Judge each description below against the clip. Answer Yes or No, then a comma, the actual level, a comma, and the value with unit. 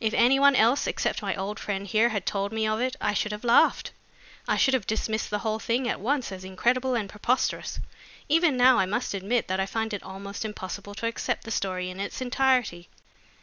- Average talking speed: No, fast, 220 wpm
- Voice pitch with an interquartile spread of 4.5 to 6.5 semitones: No, average, 3.7 semitones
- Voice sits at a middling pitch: No, high, 220 Hz